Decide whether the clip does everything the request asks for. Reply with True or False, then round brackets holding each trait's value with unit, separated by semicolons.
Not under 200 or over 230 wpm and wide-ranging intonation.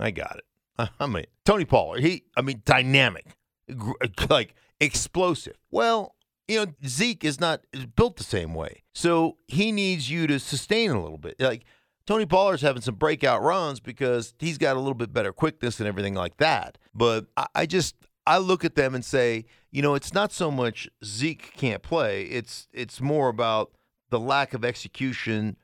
False (185 wpm; 5.9 semitones)